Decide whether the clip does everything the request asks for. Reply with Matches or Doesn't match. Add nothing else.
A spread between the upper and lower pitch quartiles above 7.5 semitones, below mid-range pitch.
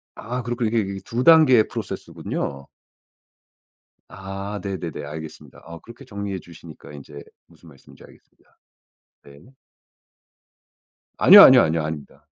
Doesn't match